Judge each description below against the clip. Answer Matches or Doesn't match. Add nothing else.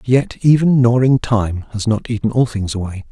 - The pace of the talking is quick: Matches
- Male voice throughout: Matches